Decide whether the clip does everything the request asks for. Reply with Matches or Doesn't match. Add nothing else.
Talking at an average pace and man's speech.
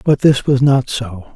Doesn't match